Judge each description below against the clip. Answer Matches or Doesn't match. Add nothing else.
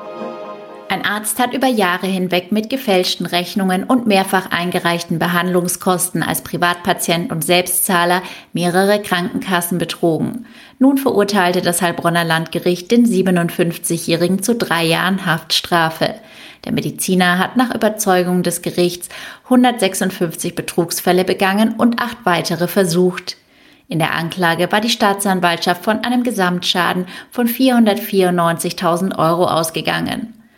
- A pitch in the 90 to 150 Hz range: Doesn't match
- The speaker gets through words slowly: Matches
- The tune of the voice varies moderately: Matches